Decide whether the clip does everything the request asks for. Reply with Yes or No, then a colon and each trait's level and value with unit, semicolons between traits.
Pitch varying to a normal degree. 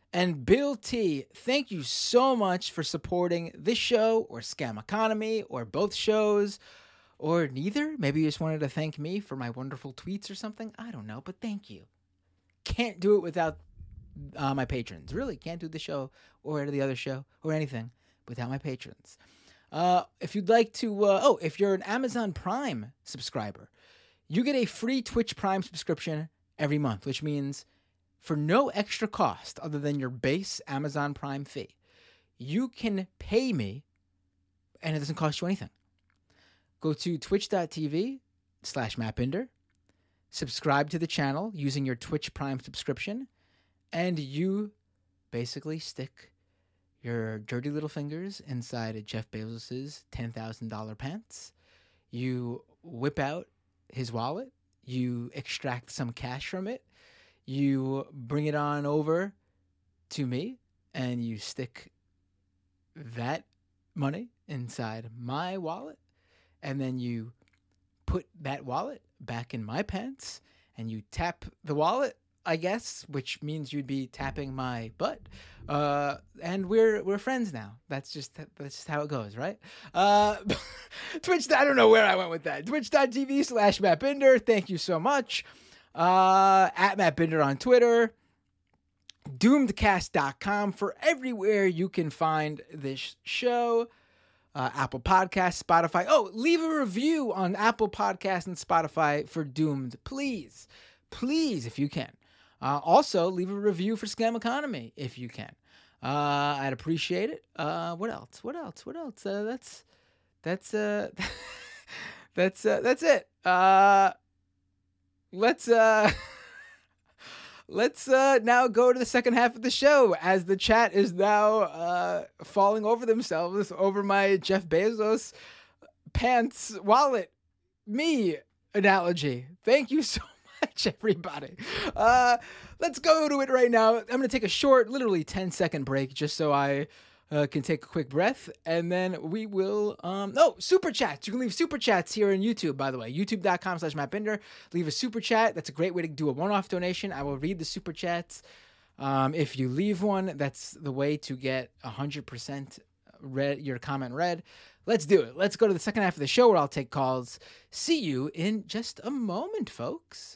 No: wide, 8.1 semitones